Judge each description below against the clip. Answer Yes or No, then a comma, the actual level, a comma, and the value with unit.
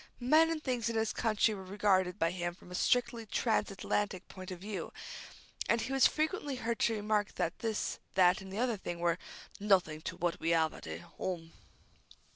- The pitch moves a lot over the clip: No, average, 4.4 semitones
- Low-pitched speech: No, high, 200 Hz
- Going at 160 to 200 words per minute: Yes, average, 195 wpm